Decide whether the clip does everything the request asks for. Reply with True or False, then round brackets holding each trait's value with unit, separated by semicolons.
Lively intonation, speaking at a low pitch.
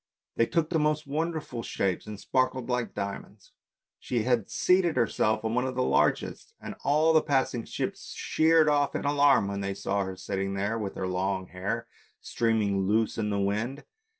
True (6.2 semitones; 115 Hz)